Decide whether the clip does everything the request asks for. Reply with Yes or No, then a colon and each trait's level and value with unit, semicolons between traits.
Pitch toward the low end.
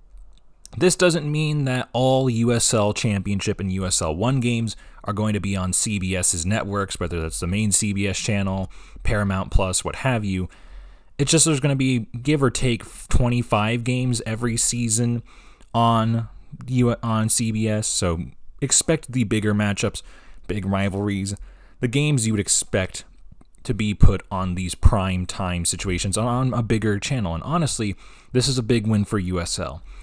Yes: low, 105 Hz